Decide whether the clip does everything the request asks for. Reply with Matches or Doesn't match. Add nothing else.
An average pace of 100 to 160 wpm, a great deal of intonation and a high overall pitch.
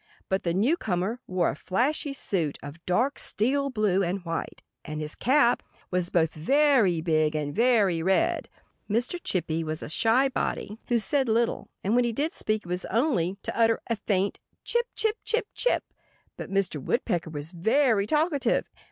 Doesn't match